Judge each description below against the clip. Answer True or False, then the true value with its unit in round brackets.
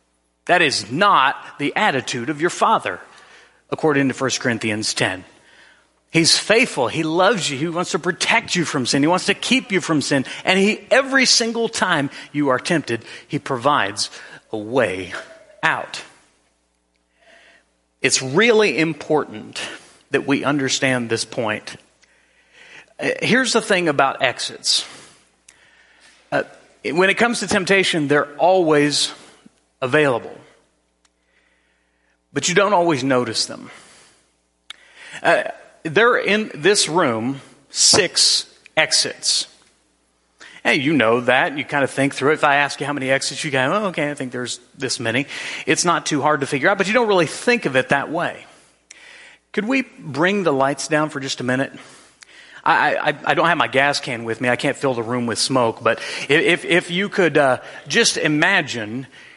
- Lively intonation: True (6.5 semitones)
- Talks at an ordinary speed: True (160 wpm)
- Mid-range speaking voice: True (145 Hz)